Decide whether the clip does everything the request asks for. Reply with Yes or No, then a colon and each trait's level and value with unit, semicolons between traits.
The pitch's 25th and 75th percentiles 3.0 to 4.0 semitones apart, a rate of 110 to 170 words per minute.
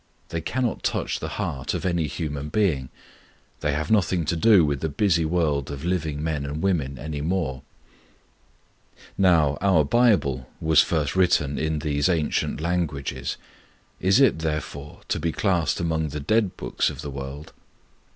Yes: average, 3.5 semitones; average, 160 wpm